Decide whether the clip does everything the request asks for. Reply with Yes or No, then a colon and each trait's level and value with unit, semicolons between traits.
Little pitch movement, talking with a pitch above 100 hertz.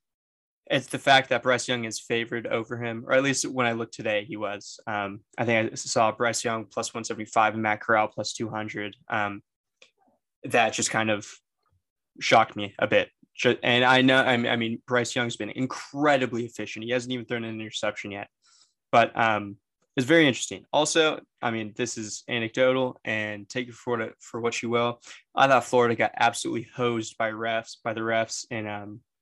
Yes: narrow, 2.2 semitones; low, 115 Hz